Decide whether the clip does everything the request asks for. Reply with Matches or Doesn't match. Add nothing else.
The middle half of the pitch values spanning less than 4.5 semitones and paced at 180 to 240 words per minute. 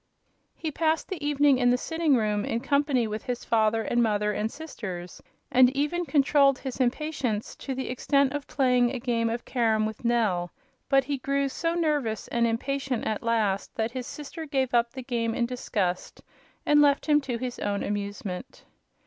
Matches